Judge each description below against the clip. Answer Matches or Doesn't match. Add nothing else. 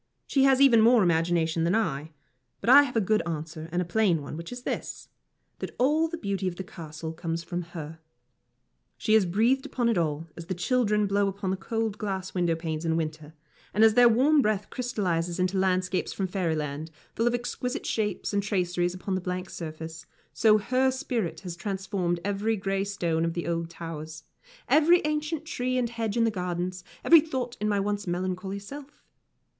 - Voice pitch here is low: Doesn't match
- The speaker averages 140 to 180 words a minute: Doesn't match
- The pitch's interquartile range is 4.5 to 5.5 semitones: Matches